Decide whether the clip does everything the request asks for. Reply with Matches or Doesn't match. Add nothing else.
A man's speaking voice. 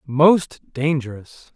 Matches